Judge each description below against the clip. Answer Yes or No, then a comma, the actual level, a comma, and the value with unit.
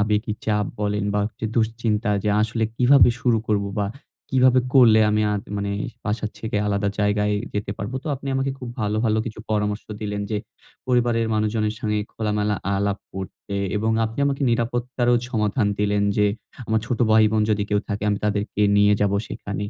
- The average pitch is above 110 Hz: No, low, 105 Hz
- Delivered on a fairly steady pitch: Yes, narrow, 1.9 semitones